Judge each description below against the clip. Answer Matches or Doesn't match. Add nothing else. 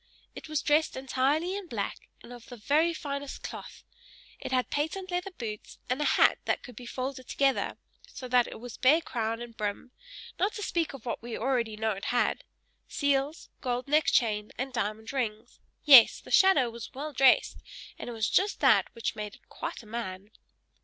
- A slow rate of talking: Doesn't match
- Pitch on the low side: Doesn't match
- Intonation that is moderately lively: Matches